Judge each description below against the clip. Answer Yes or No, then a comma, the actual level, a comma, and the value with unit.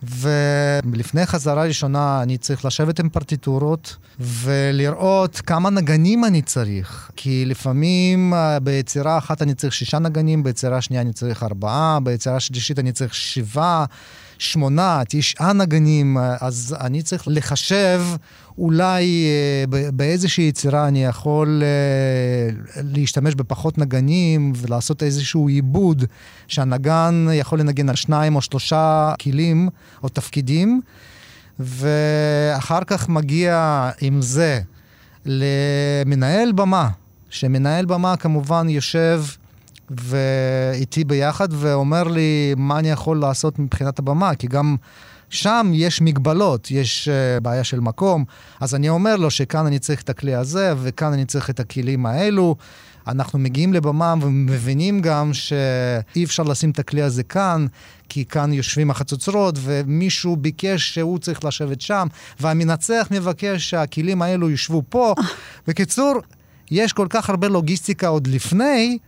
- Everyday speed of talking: Yes, average, 120 wpm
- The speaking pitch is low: No, medium, 145 Hz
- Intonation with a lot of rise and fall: No, average, 3.8 semitones